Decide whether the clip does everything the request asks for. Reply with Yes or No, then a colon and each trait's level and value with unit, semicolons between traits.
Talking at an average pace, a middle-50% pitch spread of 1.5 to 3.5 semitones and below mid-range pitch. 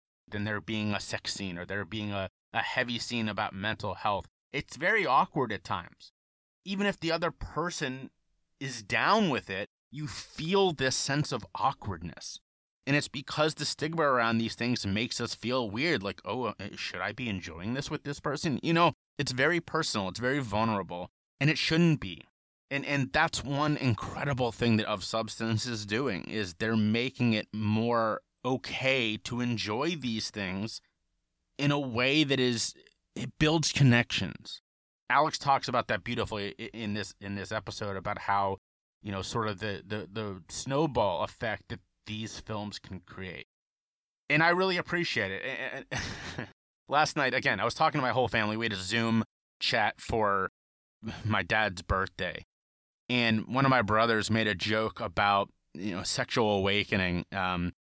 No: average, 170 wpm; average, 4.8 semitones; low, 115 Hz